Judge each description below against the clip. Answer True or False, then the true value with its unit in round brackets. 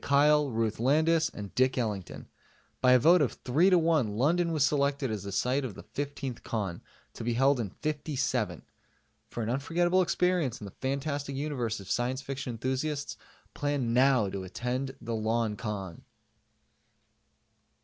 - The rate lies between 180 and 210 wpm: False (155 wpm)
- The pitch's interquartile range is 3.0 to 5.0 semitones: True (4.2 semitones)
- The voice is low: True (130 Hz)